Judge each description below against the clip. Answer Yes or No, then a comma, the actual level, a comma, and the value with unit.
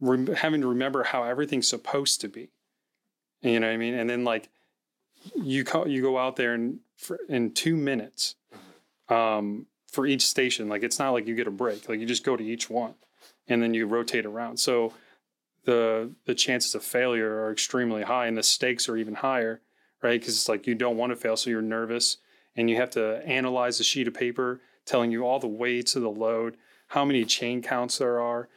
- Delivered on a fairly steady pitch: Yes, narrow, 1.9 semitones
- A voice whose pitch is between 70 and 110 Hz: No, low, 120 Hz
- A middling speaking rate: No, fast, 210 wpm